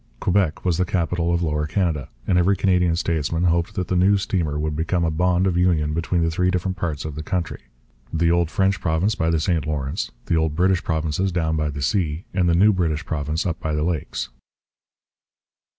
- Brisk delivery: Yes, fast, 210 wpm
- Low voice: Yes, very low, 85 Hz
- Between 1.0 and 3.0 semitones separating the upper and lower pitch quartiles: Yes, average, 2.7 semitones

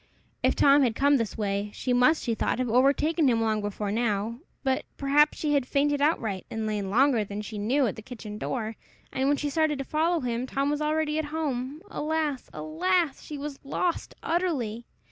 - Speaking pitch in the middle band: No, very high, 270 Hz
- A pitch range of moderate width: Yes, average, 5.0 semitones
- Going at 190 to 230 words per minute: Yes, average, 200 wpm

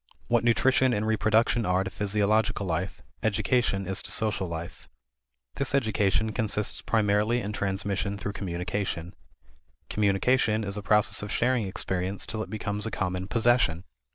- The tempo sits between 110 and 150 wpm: Yes, average, 145 wpm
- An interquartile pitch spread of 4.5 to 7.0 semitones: No, narrow, 2.4 semitones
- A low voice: Yes, low, 105 Hz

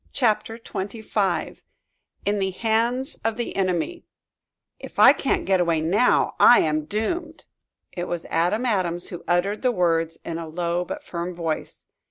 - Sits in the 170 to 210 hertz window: Yes, high, 190 Hz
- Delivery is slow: No, average, 155 wpm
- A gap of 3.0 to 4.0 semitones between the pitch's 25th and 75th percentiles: No, average, 4.9 semitones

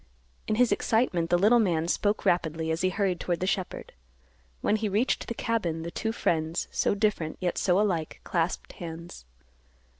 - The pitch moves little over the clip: No, average, 4.1 semitones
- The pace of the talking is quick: No, average, 175 wpm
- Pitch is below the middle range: No, medium, 180 Hz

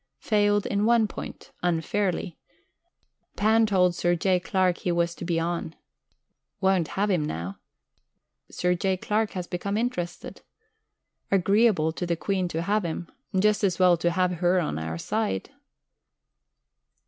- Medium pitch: Yes, medium, 180 Hz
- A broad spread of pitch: No, average, 3.1 semitones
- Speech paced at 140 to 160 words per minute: Yes, average, 145 wpm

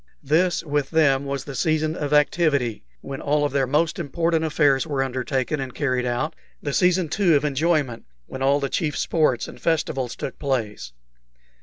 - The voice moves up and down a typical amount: Yes, average, 3.0 semitones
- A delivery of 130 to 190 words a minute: Yes, average, 170 wpm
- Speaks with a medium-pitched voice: Yes, medium, 145 Hz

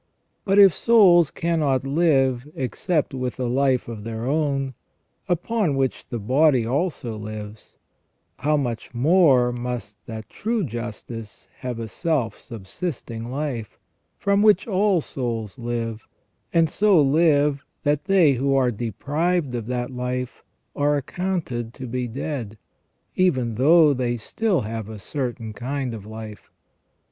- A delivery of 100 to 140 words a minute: Yes, slow, 135 wpm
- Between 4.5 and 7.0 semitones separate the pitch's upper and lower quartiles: Yes, average, 5.1 semitones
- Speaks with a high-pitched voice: No, low, 130 Hz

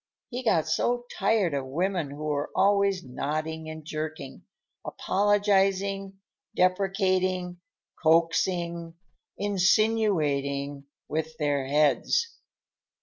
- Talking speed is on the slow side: Yes, slow, 90 wpm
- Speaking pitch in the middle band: Yes, medium, 170 Hz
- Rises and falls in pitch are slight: No, average, 4.3 semitones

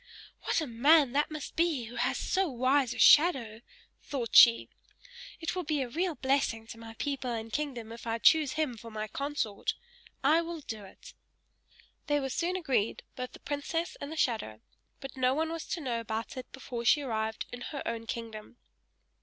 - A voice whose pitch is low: No, very high, 260 Hz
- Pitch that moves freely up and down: No, average, 4.7 semitones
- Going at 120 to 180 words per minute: No, average, 190 wpm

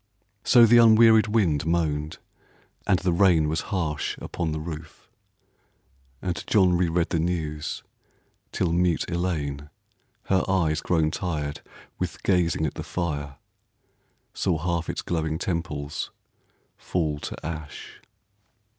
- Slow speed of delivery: Yes, slow, 120 wpm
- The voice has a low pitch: Yes, very low, 85 Hz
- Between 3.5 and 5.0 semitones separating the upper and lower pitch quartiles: No, average, 2.8 semitones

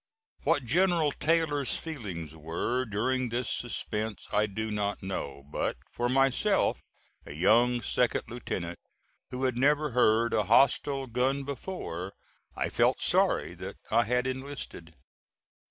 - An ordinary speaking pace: No, slow, 130 wpm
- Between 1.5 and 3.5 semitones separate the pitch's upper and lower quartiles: No, average, 4.4 semitones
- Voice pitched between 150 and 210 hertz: No, low, 120 Hz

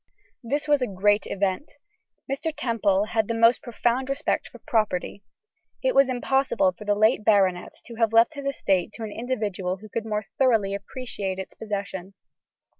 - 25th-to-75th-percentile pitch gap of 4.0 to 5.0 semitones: Yes, average, 4.3 semitones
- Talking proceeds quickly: No, average, 170 wpm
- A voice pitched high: Yes, high, 220 Hz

